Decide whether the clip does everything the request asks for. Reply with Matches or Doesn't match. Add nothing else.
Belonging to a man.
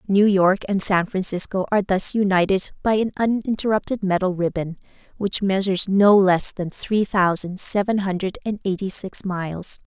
Doesn't match